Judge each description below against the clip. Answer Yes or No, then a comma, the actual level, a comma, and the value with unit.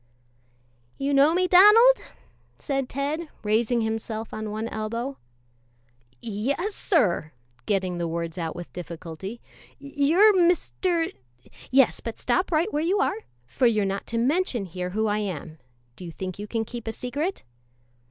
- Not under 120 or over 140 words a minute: No, average, 150 wpm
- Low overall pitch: No, high, 230 Hz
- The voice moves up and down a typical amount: No, wide, 7.8 semitones